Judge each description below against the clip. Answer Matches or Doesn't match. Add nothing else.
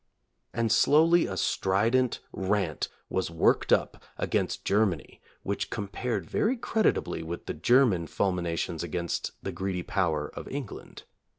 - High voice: Doesn't match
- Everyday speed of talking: Doesn't match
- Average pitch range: Doesn't match